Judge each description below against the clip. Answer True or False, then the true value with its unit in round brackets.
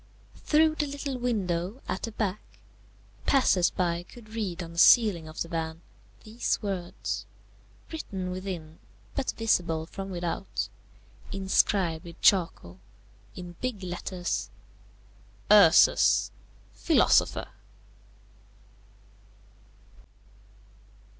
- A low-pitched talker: False (185 Hz)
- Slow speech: True (95 wpm)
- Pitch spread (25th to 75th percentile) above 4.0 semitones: True (4.6 semitones)